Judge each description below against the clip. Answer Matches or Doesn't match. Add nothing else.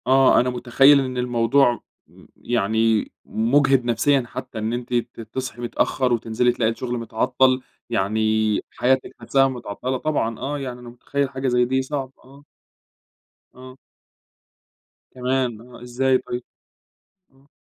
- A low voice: Matches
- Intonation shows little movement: Matches